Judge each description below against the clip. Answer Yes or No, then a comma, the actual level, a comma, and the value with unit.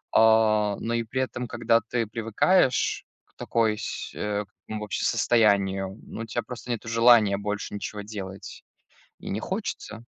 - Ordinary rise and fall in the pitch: No, narrow, 2.1 semitones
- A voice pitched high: No, low, 110 Hz